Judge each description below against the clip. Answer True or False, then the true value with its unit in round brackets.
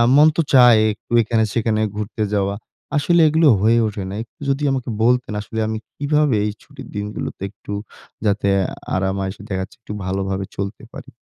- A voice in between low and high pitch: False (110 Hz)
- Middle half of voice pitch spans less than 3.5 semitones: False (4.1 semitones)